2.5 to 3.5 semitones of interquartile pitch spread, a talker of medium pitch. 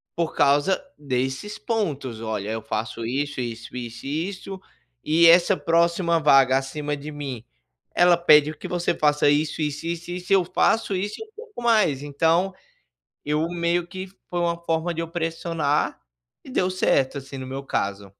No: average, 4.4 semitones; medium, 155 Hz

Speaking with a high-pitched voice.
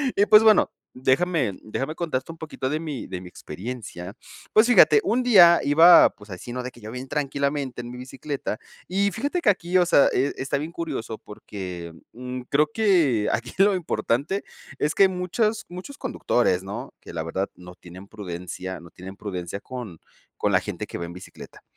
No: low, 130 Hz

